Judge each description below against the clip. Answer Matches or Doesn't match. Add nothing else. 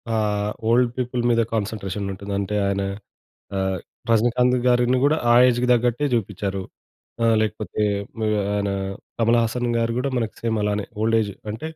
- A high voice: Doesn't match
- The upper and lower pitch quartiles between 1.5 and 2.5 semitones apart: Doesn't match